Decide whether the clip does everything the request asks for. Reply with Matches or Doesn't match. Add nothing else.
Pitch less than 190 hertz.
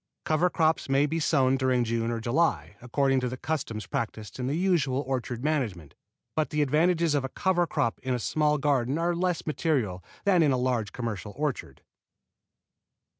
Matches